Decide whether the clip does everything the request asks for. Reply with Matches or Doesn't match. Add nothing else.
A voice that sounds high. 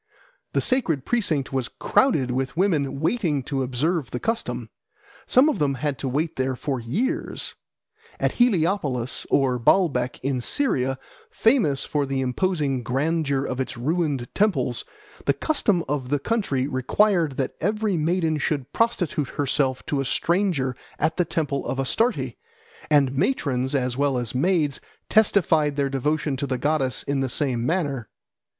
Doesn't match